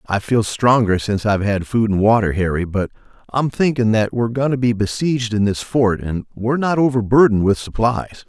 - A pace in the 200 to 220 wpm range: Yes, fast, 205 wpm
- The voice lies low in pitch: Yes, low, 110 Hz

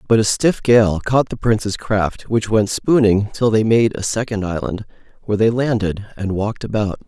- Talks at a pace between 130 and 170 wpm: No, average, 195 wpm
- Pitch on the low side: Yes, low, 110 Hz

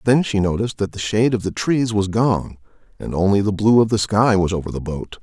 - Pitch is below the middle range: Yes, low, 100 Hz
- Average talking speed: No, fast, 255 wpm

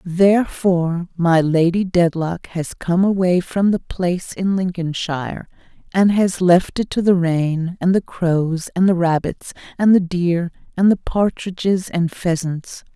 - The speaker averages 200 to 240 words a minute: No, average, 155 wpm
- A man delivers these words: No, female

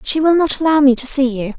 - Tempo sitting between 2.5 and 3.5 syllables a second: No, 6.1 syllables/s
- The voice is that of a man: No, female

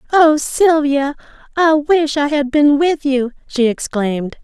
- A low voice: No, very high, 285 Hz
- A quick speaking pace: No, average, 150 wpm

